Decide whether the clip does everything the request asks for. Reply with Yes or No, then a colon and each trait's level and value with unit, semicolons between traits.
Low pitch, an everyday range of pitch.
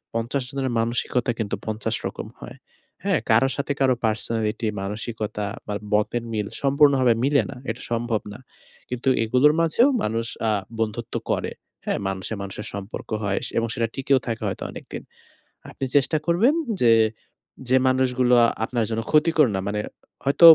Yes: low, 120 Hz; average, 3.7 semitones